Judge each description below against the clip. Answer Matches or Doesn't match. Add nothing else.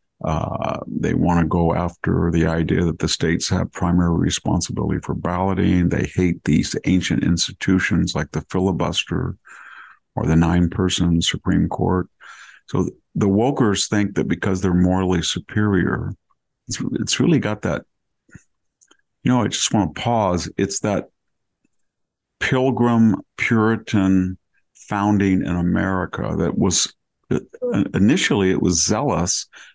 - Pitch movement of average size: Doesn't match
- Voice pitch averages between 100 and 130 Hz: Doesn't match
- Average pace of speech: Doesn't match